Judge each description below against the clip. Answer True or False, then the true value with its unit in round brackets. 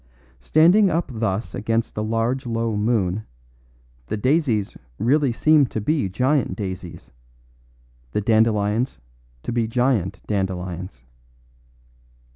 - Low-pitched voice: True (115 Hz)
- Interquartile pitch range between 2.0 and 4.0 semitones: False (4.4 semitones)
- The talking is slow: True (105 wpm)